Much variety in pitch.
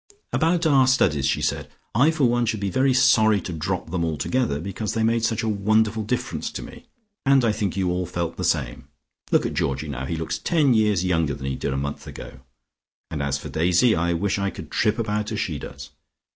Yes: wide, 6.3 semitones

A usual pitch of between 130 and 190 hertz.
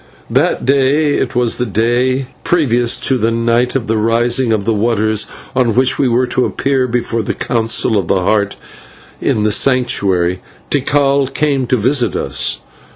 No: low, 120 Hz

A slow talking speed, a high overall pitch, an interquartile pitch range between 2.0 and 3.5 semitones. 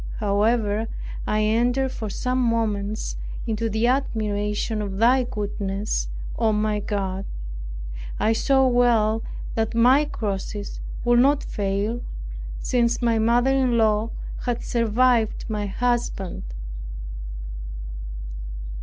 Yes: slow, 105 wpm; high, 225 Hz; narrow, 2.5 semitones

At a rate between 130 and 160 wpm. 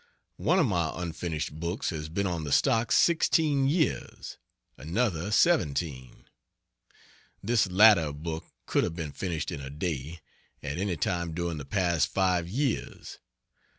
Yes: average, 140 wpm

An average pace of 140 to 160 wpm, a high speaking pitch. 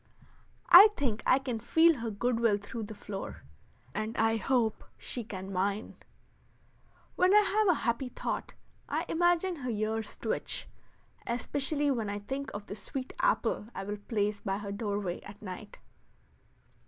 Yes: average, 155 wpm; high, 225 Hz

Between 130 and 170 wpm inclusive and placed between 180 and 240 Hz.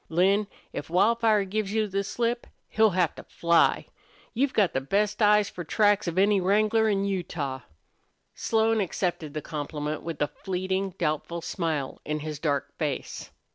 Yes: average, 160 wpm; high, 190 Hz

